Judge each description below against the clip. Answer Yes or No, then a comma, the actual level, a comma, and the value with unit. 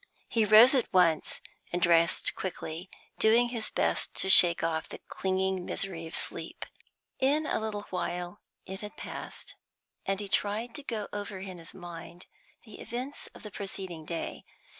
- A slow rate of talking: No, average, 160 wpm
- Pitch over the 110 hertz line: Yes, high, 190 Hz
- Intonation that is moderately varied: Yes, average, 3.8 semitones